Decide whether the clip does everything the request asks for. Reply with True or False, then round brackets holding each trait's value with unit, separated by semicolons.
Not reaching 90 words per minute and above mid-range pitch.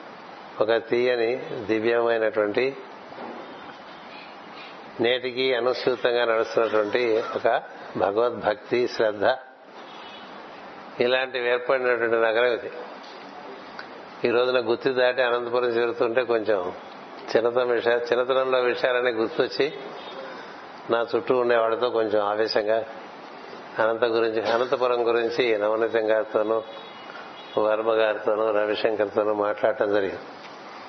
False (80 wpm; 115 Hz)